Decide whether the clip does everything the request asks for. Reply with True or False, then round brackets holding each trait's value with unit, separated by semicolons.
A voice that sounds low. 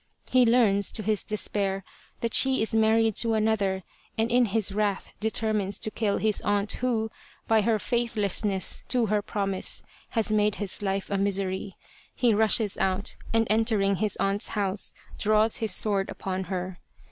False (210 Hz)